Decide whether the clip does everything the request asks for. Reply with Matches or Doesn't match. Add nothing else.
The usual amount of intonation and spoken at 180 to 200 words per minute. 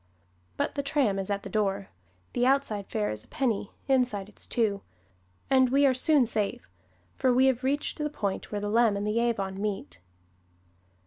Matches